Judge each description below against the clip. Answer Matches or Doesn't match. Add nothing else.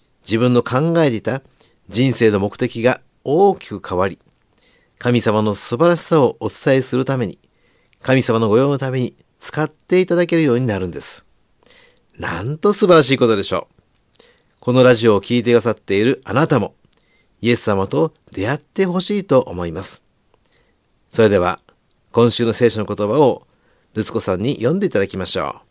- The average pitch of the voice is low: Matches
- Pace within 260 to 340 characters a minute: Matches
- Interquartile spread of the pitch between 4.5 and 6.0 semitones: Matches